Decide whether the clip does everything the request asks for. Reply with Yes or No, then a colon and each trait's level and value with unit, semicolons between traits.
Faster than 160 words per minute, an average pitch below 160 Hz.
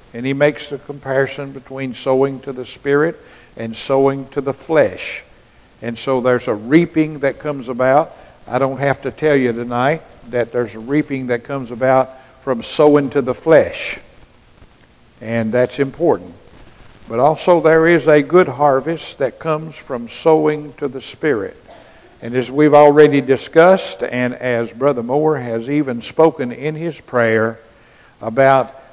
No: average, 155 wpm; low, 135 Hz